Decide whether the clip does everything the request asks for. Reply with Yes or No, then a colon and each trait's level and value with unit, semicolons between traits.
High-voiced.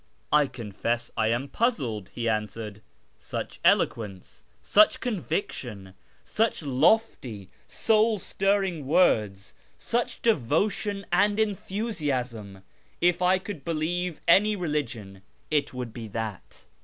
No: medium, 145 Hz